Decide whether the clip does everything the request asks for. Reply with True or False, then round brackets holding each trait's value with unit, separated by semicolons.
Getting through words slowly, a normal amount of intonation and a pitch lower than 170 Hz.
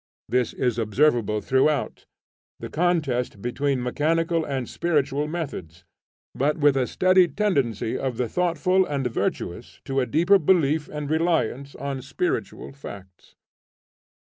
True (125 wpm; 4.8 semitones; 140 Hz)